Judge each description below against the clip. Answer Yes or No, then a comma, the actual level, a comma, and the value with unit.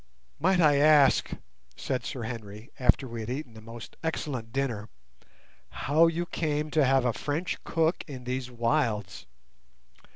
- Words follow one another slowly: No, average, 150 wpm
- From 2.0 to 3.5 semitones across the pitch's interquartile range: No, average, 4.6 semitones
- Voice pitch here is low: Yes, low, 130 Hz